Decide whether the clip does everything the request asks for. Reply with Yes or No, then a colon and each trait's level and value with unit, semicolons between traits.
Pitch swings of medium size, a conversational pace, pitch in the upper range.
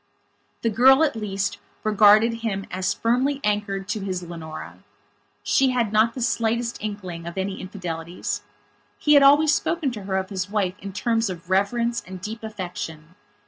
Yes: average, 3.7 semitones; average, 165 wpm; high, 210 Hz